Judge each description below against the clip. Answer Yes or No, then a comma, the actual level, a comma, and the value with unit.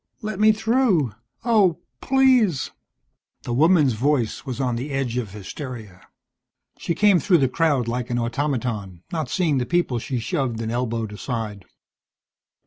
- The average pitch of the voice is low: Yes, low, 130 Hz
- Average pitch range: No, wide, 6.7 semitones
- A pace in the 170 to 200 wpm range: No, average, 150 wpm